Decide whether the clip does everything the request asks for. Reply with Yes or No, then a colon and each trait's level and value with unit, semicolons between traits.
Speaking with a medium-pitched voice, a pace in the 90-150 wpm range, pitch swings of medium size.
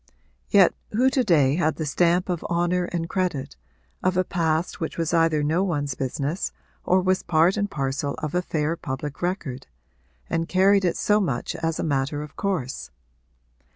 No: medium, 165 Hz; average, 175 wpm; average, 3.7 semitones